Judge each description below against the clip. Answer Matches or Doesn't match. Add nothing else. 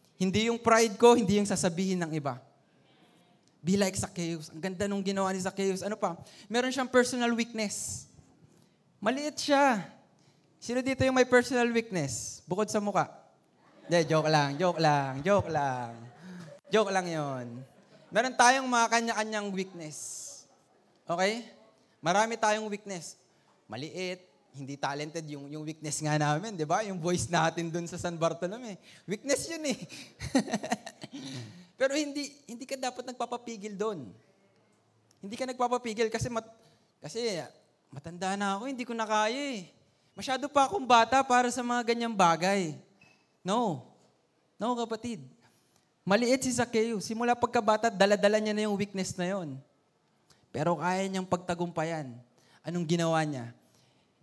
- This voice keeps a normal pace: Matches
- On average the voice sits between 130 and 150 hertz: Doesn't match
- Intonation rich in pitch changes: Matches